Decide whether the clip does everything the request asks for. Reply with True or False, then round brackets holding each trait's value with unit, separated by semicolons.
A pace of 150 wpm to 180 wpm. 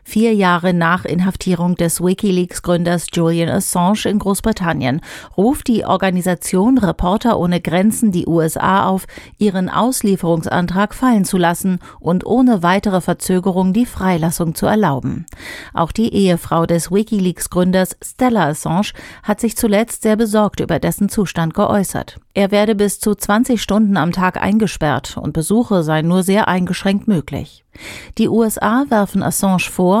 False (140 wpm)